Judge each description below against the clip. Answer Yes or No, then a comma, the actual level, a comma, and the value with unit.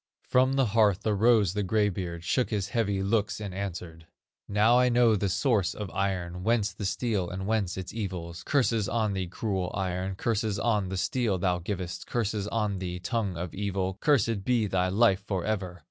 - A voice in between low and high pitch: No, low, 100 Hz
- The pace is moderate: Yes, average, 185 wpm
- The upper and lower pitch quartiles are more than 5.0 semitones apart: No, average, 3.2 semitones